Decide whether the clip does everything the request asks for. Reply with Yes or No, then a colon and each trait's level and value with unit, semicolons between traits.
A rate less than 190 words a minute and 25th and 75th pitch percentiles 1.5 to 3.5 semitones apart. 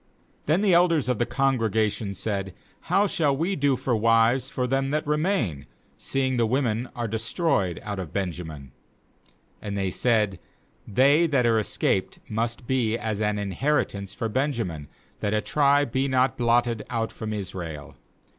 No: average, 165 wpm; average, 4.6 semitones